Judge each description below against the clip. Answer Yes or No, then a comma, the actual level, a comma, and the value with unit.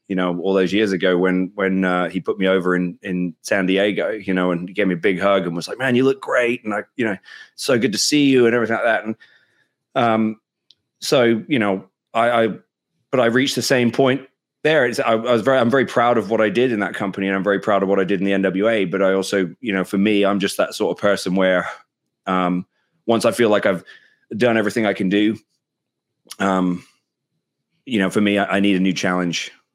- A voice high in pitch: No, low, 100 Hz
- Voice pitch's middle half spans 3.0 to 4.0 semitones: Yes, average, 3.3 semitones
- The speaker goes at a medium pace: No, fast, 245 wpm